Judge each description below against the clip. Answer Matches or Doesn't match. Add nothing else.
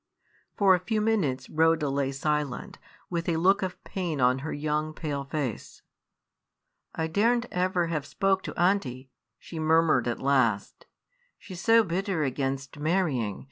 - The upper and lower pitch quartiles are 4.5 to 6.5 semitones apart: Matches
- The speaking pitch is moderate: Matches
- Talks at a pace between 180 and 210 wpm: Doesn't match